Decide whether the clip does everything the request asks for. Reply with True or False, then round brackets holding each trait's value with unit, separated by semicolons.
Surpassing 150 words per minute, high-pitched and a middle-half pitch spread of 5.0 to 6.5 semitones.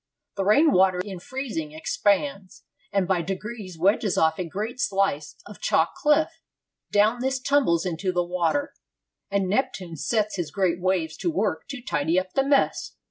True (165 wpm; 195 Hz; 5.4 semitones)